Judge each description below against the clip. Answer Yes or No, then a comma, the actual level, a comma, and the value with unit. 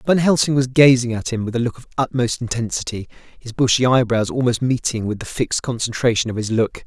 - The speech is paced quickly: Yes, fast, 210 wpm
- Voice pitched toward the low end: Yes, low, 120 Hz